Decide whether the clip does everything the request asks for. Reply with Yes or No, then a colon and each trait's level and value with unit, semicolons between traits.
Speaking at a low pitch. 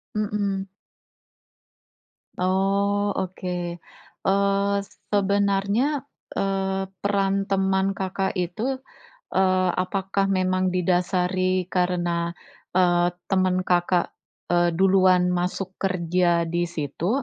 No: high, 190 Hz